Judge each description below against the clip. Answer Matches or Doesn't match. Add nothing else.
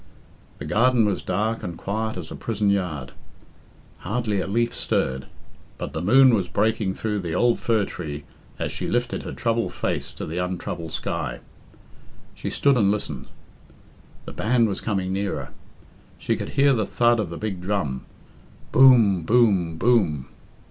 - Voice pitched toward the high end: Doesn't match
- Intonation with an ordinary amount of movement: Matches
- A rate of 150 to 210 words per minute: Matches